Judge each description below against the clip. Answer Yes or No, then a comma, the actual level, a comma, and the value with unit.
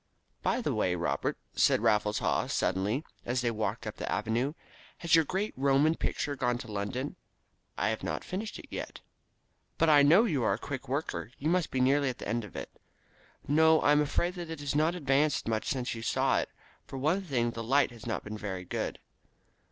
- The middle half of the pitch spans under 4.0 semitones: No, wide, 5.5 semitones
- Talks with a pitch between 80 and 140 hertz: Yes, low, 135 Hz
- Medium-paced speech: No, fast, 215 wpm